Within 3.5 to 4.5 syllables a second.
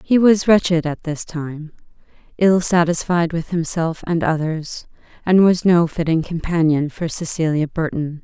Yes: 4.4 syllables/s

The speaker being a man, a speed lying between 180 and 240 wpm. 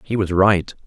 Yes: male; fast, 205 wpm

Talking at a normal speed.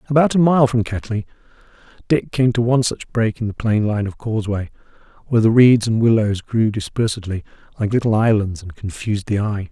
Yes: average, 190 wpm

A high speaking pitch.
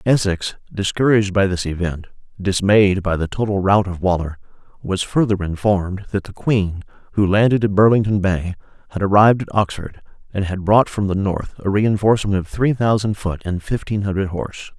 No: low, 100 Hz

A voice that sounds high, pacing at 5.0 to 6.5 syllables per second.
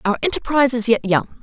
Yes: high, 240 Hz; 6.4 syllables/s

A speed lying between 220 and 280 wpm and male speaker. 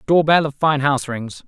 Yes: fast, 245 wpm; male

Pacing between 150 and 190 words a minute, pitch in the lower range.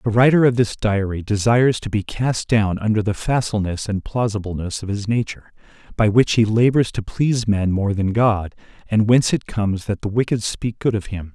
No: fast, 205 wpm; low, 110 Hz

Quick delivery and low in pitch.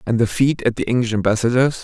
Yes: fast, 230 wpm; low, 120 Hz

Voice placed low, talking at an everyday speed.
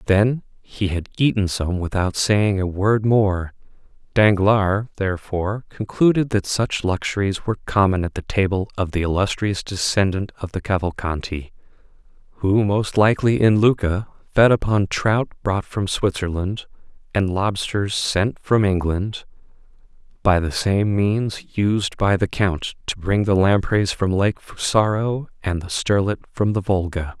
Yes: low, 100 Hz; average, 145 wpm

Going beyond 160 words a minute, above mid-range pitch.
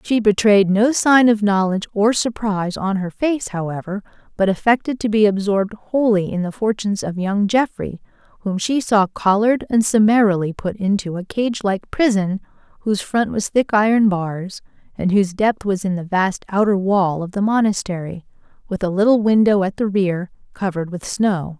Yes: average, 180 wpm; high, 205 Hz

